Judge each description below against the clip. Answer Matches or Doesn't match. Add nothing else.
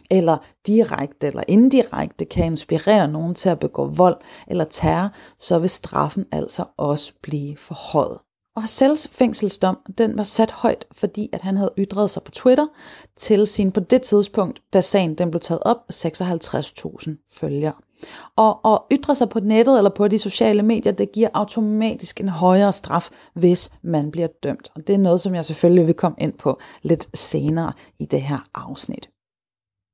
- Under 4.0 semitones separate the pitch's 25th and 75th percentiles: Doesn't match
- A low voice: Doesn't match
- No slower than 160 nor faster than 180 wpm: Matches